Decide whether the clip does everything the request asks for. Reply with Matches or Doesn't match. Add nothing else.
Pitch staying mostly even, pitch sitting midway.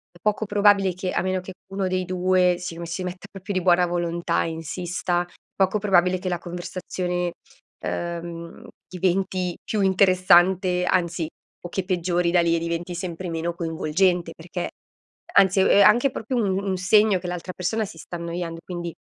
Matches